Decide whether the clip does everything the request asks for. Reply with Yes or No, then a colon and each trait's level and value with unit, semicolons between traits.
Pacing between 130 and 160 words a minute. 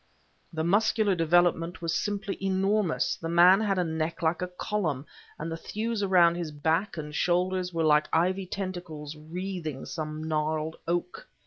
Yes: average, 155 wpm